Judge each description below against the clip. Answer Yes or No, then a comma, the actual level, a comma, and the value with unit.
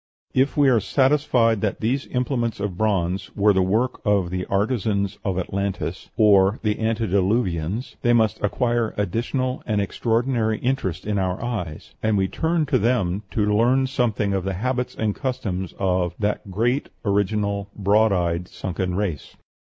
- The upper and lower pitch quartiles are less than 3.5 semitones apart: No, average, 3.9 semitones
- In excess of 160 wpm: No, average, 155 wpm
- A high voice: No, low, 105 Hz